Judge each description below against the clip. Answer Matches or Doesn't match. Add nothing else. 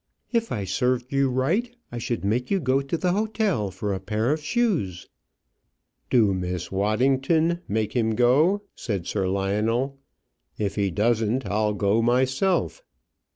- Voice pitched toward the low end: Matches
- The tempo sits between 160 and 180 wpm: Doesn't match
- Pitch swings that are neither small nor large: Doesn't match